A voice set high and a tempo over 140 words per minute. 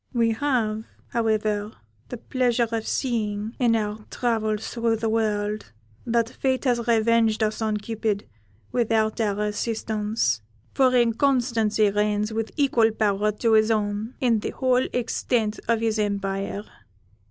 No: high, 220 Hz; slow, 135 wpm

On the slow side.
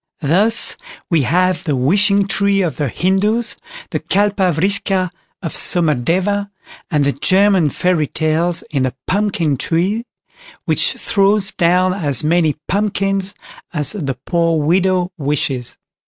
Yes: slow, 130 wpm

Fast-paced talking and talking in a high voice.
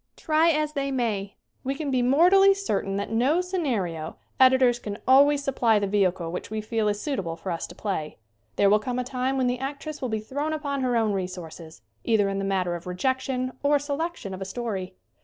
Yes: fast, 215 wpm; high, 245 Hz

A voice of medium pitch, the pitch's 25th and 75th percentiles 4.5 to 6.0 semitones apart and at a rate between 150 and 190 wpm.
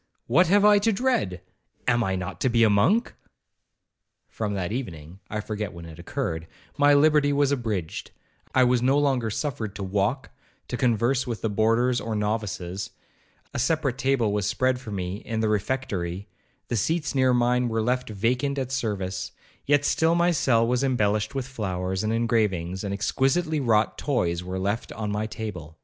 No: low, 115 Hz; average, 5.0 semitones; average, 165 wpm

